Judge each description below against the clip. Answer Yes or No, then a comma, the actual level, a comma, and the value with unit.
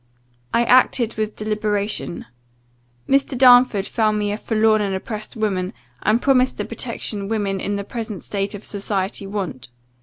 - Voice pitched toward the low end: No, high, 215 Hz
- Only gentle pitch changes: Yes, narrow, 2.1 semitones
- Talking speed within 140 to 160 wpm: Yes, average, 150 wpm